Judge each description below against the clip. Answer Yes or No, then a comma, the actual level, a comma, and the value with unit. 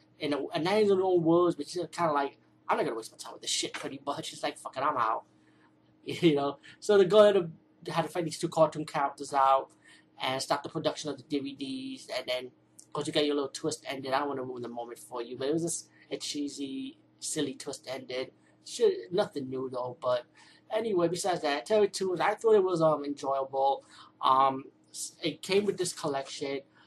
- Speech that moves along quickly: Yes, fast, 225 wpm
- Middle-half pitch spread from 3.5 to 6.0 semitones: Yes, average, 4.7 semitones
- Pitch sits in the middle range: Yes, medium, 150 Hz